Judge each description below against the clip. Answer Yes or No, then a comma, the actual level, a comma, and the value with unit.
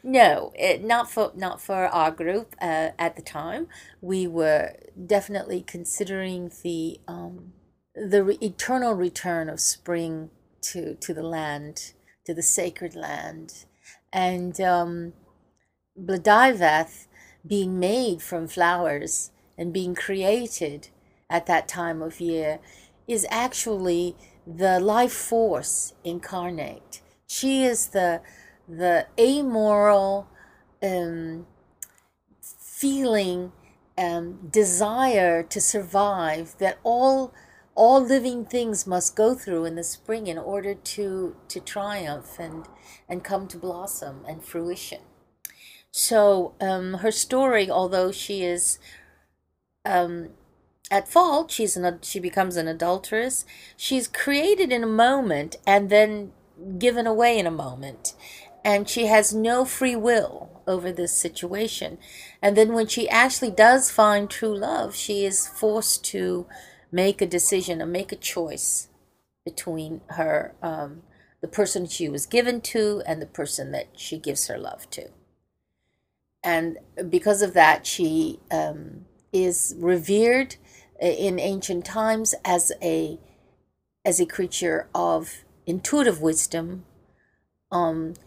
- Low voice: No, high, 190 Hz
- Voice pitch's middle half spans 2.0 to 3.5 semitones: No, average, 4.3 semitones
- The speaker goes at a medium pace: No, slow, 125 wpm